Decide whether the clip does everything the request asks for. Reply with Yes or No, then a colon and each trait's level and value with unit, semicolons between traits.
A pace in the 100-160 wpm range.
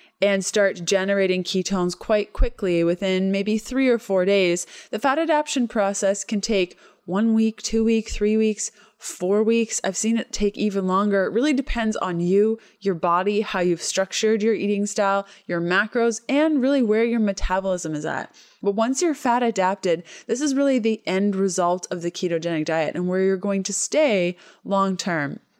No: average, 180 wpm